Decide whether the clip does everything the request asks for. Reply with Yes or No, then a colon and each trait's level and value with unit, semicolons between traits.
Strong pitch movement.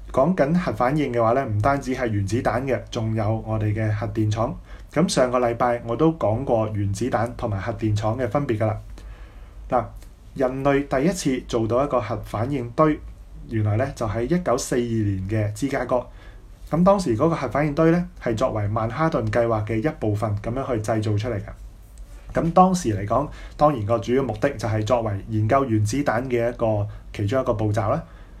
No: average, 3.7 semitones